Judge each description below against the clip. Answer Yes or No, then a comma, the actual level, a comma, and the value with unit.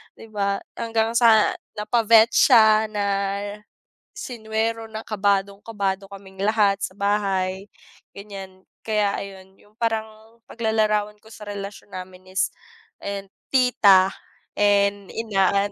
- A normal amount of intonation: No, narrow, 1.9 semitones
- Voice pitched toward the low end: No, high, 205 Hz